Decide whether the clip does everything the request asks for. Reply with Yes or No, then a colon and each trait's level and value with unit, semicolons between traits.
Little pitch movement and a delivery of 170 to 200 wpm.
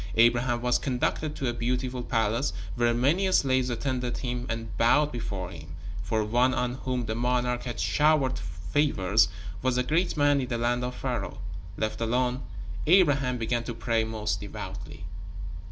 No: narrow, 2.2 semitones; average, 160 wpm